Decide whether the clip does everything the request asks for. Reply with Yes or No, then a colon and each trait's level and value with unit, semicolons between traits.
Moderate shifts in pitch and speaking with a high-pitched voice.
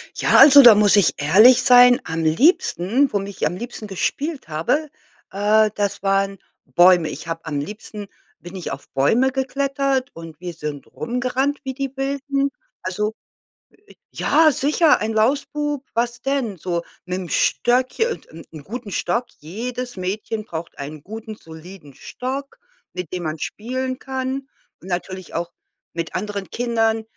No: wide, 6.8 semitones; high, 215 Hz